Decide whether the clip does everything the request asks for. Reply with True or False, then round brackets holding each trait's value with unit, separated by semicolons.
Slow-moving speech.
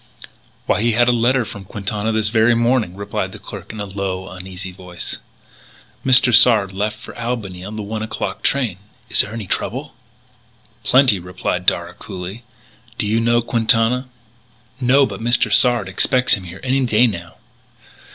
False (165 wpm)